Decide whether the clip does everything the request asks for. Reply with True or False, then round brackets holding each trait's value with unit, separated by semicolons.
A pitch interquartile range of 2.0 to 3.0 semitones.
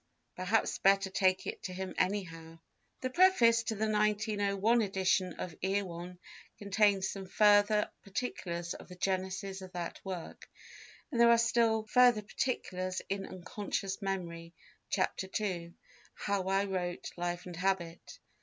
True (2.6 semitones)